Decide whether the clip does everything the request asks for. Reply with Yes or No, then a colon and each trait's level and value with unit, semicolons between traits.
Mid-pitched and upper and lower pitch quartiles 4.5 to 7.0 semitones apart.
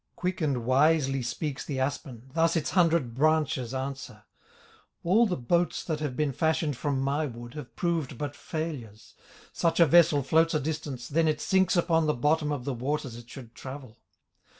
No: medium, 145 Hz; average, 3.7 semitones